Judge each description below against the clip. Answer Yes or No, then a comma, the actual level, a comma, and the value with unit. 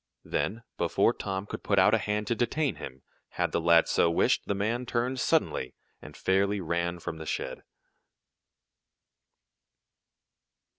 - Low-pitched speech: Yes, low, 100 Hz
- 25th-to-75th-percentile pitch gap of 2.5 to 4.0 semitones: No, average, 4.8 semitones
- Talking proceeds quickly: No, average, 145 wpm